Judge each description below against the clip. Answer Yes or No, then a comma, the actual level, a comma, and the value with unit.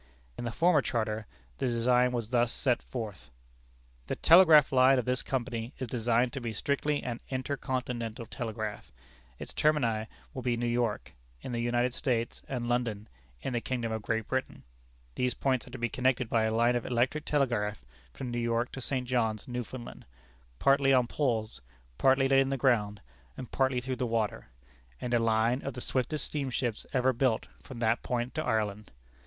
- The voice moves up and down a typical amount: No, narrow, 2.2 semitones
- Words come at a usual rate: Yes, average, 180 wpm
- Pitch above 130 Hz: No, low, 120 Hz